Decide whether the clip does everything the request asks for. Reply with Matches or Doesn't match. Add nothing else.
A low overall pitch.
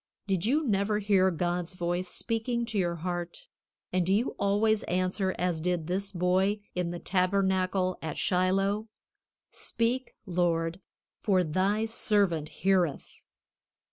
Doesn't match